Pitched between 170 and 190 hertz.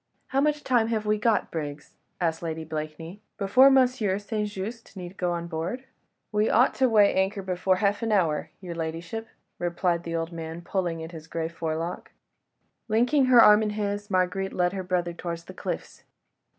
Yes: medium, 185 Hz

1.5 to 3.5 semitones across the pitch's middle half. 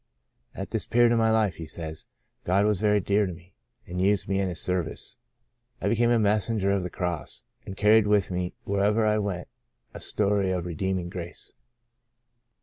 Yes: average, 2.9 semitones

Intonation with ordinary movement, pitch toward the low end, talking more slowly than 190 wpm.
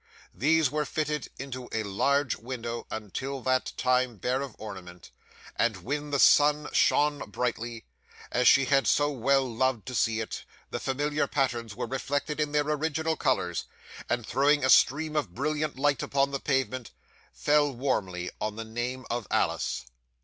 Yes: average, 3.8 semitones; low, 130 Hz; average, 160 wpm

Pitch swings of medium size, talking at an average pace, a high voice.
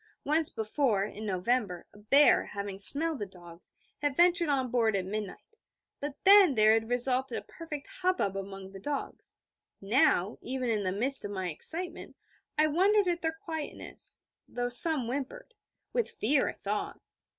No: wide, 7.2 semitones; average, 160 wpm; very high, 250 Hz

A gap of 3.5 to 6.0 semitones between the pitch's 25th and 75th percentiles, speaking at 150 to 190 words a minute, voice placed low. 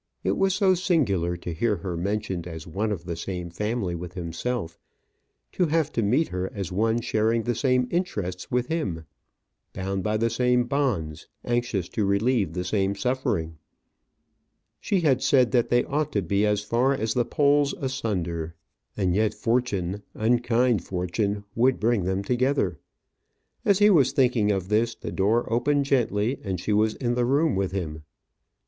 Yes: average, 5.1 semitones; average, 170 wpm; low, 110 Hz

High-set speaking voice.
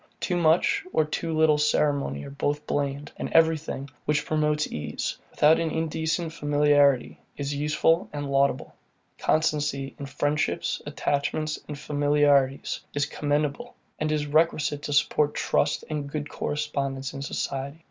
No: medium, 145 Hz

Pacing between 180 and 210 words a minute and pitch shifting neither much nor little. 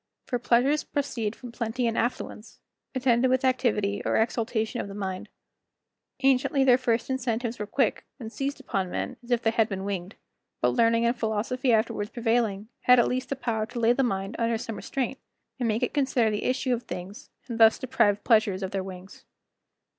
Yes: average, 190 wpm; average, 3.0 semitones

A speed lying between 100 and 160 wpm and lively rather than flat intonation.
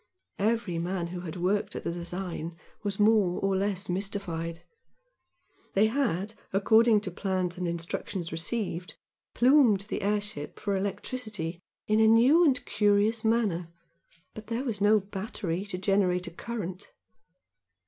No: average, 140 wpm; average, 3.5 semitones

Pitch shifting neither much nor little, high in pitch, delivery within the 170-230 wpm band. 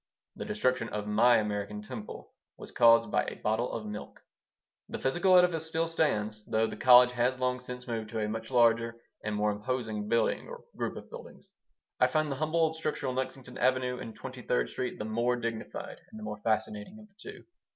No: average, 3.5 semitones; low, 120 Hz; fast, 205 wpm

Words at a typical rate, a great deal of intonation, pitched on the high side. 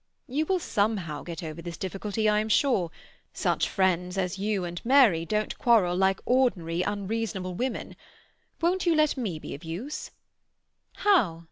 Yes: average, 155 wpm; wide, 5.7 semitones; high, 200 Hz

